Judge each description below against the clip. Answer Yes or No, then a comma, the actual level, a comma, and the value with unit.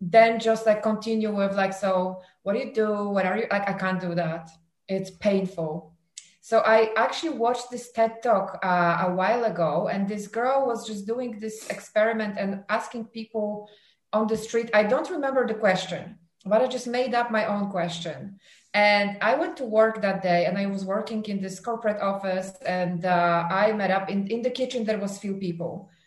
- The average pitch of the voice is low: No, high, 205 Hz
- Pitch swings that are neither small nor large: Yes, average, 3.1 semitones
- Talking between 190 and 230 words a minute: Yes, average, 200 wpm